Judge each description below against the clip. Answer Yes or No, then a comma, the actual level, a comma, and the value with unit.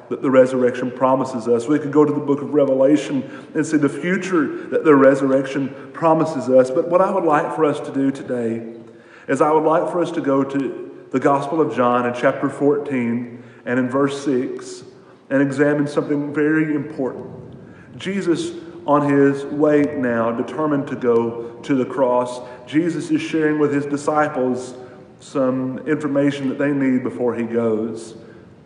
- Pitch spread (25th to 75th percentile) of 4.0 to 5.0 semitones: No, average, 3.2 semitones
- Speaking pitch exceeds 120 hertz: Yes, medium, 140 Hz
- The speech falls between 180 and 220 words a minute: No, average, 170 wpm